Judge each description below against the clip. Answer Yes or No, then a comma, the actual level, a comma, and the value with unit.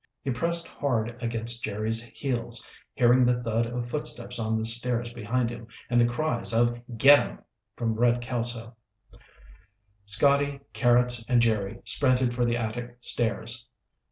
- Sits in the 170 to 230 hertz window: No, low, 120 Hz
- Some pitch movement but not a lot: No, narrow, 1.2 semitones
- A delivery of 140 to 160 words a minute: Yes, average, 145 wpm